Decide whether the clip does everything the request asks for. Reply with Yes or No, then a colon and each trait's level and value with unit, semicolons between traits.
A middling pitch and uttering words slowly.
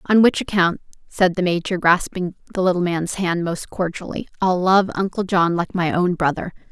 No: medium, 180 Hz; average, 190 wpm